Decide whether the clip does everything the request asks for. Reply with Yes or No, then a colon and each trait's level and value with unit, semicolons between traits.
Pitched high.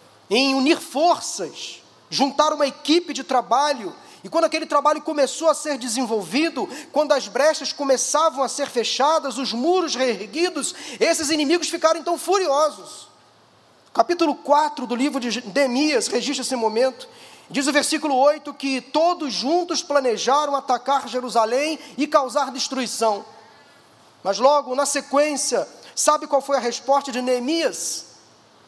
Yes: very high, 285 Hz